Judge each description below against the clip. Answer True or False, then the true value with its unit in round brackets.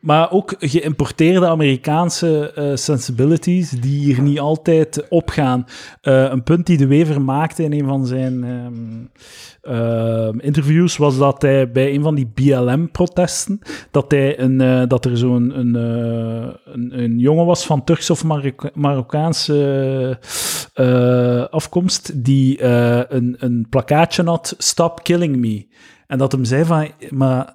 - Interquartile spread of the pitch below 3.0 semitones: False (3.8 semitones)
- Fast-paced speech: False (150 wpm)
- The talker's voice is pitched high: False (140 Hz)